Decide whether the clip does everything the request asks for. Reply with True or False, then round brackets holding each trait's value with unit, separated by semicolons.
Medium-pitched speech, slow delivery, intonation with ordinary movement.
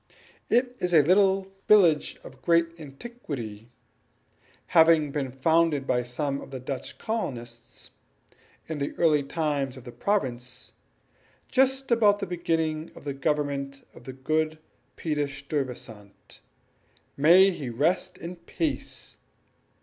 True (150 Hz; 125 wpm; 4.6 semitones)